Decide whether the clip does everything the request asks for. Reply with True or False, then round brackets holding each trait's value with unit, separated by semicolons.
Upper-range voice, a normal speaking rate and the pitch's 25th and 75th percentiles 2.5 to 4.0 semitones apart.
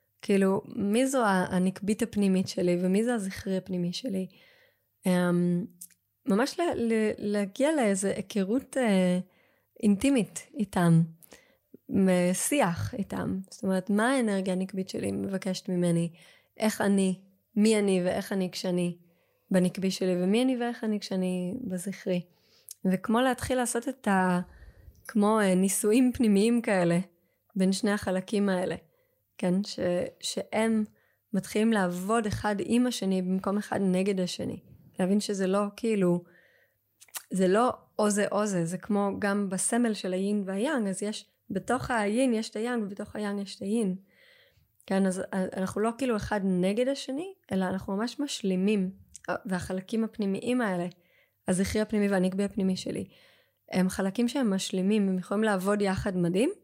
True (200 Hz; 135 wpm; 3.2 semitones)